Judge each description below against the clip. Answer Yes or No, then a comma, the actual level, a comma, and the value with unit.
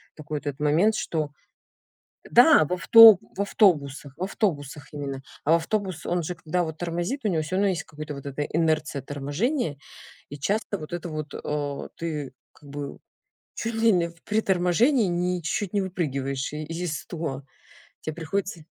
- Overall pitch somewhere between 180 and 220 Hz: No, medium, 165 Hz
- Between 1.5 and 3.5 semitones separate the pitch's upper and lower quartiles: No, average, 4.3 semitones